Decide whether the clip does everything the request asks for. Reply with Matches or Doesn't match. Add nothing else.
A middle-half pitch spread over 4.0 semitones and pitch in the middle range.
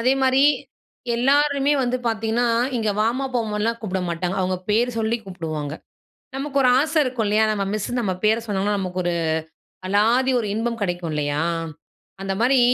Doesn't match